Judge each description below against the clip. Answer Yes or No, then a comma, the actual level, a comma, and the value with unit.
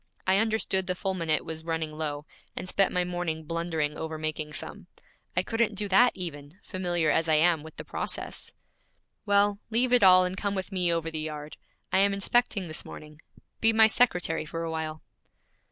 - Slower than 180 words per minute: No, average, 185 wpm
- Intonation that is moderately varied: Yes, average, 3.8 semitones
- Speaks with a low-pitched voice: No, medium, 175 Hz